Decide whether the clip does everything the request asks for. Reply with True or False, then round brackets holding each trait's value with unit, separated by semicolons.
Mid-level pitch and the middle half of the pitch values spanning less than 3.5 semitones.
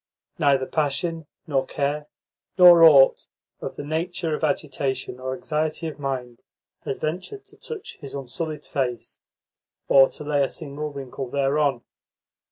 True (145 Hz; 2.7 semitones)